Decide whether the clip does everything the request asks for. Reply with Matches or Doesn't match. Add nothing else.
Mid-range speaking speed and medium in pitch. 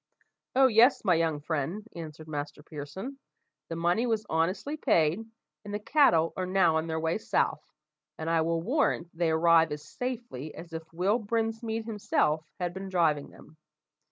Matches